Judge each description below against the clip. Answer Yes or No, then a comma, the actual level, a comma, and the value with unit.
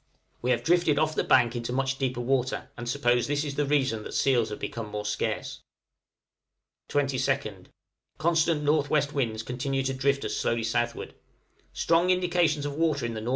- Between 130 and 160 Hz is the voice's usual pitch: Yes, low, 135 Hz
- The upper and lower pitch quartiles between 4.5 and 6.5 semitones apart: No, average, 3.7 semitones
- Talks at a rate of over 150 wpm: Yes, average, 175 wpm